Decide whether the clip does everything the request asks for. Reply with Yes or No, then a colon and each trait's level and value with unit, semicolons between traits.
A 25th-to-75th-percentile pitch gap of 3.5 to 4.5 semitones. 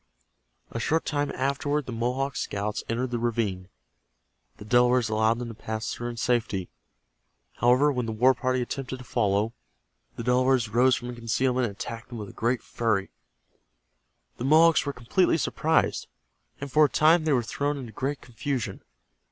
No: average, 3.0 semitones